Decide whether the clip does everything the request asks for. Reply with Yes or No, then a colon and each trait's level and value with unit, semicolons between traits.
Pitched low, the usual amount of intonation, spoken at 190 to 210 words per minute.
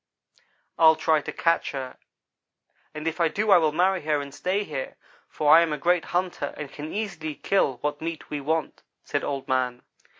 No: medium, 155 Hz; average, 3.1 semitones; average, 195 wpm